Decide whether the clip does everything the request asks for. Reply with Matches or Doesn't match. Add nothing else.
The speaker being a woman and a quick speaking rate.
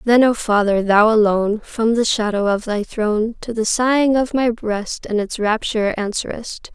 Doesn't match